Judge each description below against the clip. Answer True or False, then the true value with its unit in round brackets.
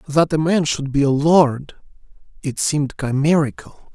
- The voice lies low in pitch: False (150 Hz)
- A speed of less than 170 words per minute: True (135 wpm)